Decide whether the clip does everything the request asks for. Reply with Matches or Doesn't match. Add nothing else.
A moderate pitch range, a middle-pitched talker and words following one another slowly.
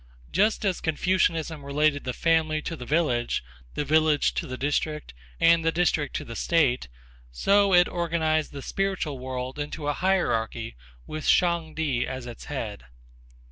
Doesn't match